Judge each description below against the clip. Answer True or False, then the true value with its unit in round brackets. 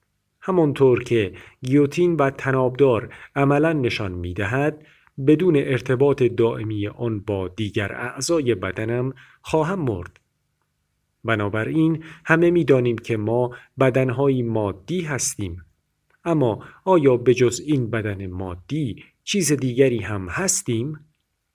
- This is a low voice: True (125 Hz)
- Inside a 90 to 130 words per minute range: True (105 wpm)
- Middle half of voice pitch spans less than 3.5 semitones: False (5.3 semitones)